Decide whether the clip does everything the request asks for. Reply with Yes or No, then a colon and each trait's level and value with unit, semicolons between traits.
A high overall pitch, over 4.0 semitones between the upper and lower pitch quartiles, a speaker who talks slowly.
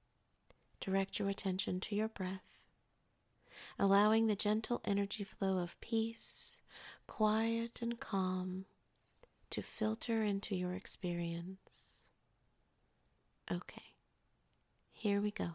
No: high, 200 Hz; average, 2.7 semitones; slow, 95 wpm